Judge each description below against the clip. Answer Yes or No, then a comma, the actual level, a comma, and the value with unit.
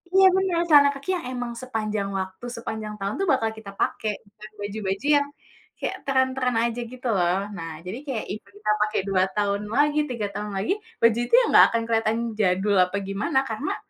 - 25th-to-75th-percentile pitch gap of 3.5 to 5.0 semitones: Yes, average, 4.5 semitones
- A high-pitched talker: Yes, high, 220 Hz